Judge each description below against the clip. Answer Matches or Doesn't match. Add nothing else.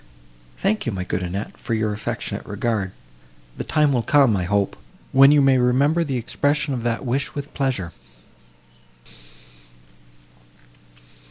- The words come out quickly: Doesn't match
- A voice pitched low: Matches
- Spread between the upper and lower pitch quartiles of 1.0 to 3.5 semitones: Doesn't match